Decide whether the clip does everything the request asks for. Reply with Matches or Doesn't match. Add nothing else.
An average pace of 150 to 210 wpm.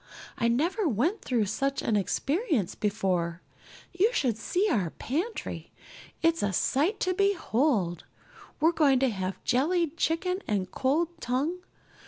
Doesn't match